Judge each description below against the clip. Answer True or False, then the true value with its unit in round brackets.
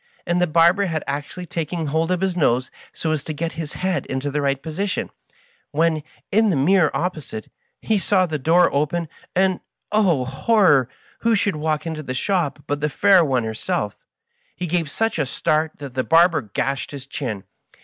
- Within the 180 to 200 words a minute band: True (195 wpm)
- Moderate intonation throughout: True (4.2 semitones)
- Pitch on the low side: False (160 Hz)